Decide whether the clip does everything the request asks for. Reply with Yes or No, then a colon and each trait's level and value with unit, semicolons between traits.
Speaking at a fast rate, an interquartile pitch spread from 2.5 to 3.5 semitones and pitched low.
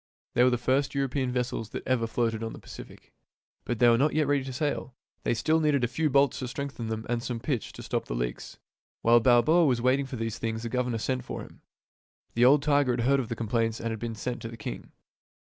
Yes: fast, 240 wpm; average, 3.1 semitones; low, 125 Hz